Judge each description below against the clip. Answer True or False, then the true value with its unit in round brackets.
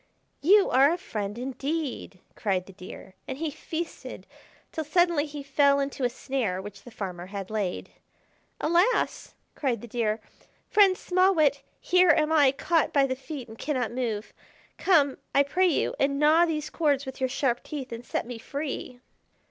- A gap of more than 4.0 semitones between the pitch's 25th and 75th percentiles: True (4.7 semitones)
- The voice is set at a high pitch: True (275 Hz)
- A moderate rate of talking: True (170 wpm)